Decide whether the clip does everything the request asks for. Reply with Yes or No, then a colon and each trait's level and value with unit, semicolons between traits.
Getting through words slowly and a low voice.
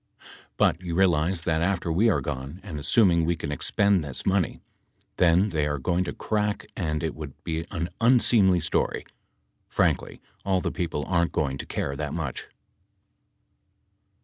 No: average, 160 wpm; very low, 85 Hz